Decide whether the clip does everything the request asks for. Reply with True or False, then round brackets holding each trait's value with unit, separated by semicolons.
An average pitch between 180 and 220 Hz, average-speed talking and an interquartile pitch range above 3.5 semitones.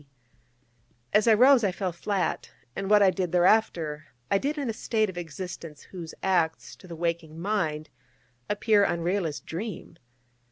True (185 Hz; 160 wpm; 4.0 semitones)